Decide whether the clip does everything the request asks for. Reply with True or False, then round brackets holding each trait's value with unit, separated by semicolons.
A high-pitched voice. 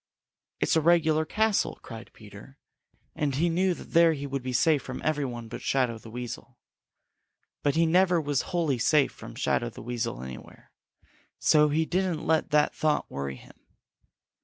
False (150 Hz)